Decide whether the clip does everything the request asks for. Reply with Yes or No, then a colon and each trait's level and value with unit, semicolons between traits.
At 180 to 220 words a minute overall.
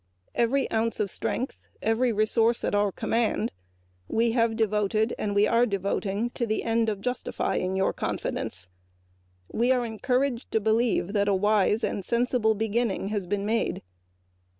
No: average, 140 wpm